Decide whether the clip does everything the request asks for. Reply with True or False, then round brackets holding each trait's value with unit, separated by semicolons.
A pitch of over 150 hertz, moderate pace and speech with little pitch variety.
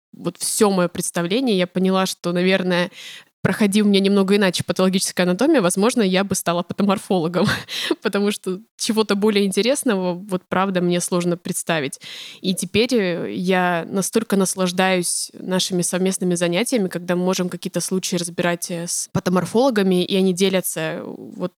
True (185 Hz; 135 wpm; 2.1 semitones)